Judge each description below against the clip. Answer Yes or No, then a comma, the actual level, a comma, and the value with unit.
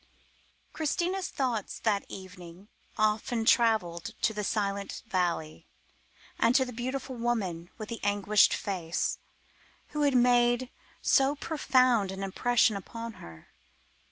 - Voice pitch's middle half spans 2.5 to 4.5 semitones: Yes, average, 4.2 semitones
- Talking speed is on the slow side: Yes, slow, 120 wpm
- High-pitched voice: Yes, high, 220 Hz